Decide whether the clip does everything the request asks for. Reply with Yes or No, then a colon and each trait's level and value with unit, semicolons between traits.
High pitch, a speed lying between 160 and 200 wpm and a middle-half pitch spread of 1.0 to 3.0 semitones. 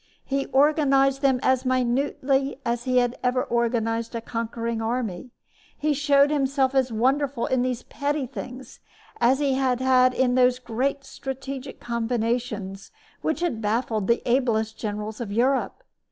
No: very high, 255 Hz; average, 140 wpm; narrow, 2.6 semitones